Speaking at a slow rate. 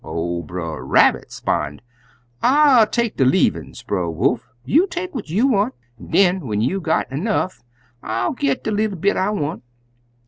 No: average, 170 wpm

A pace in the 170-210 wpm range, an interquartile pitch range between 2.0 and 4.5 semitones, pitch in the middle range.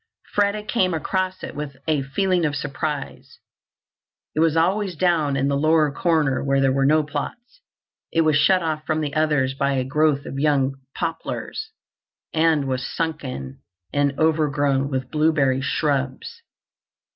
No: average, 150 wpm; average, 2.9 semitones; medium, 150 Hz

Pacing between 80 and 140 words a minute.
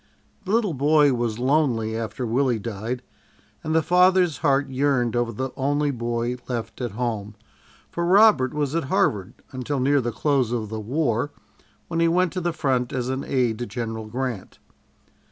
No: average, 170 wpm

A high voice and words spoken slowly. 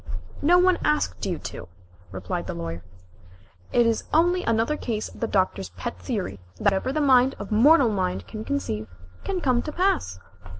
No: high, 230 Hz; average, 175 wpm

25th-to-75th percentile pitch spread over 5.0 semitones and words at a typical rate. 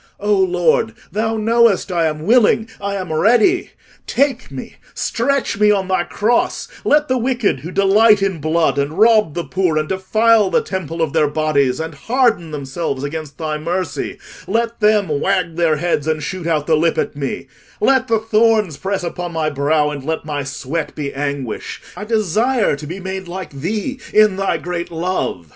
Yes: wide, 5.6 semitones; average, 175 wpm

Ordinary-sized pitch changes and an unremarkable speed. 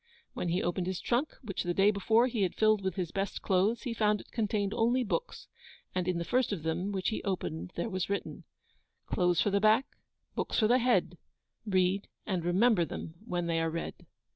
No: average, 3.8 semitones; fast, 210 wpm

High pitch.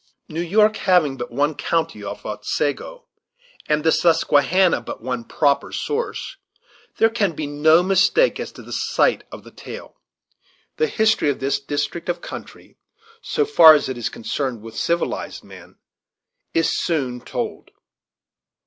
No: medium, 155 Hz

